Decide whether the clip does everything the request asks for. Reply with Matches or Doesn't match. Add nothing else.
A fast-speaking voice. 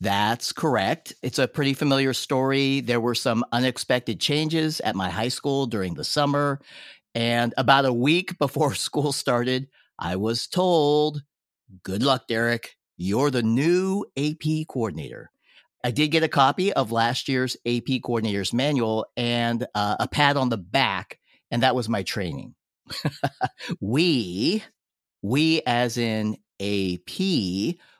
Doesn't match